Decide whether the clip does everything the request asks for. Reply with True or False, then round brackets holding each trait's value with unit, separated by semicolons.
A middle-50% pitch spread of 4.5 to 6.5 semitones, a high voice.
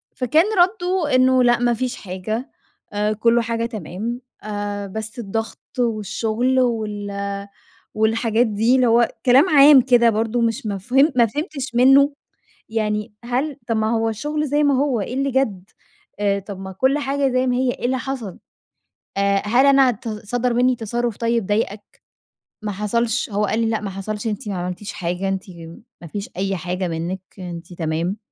False (3.8 semitones; 230 Hz)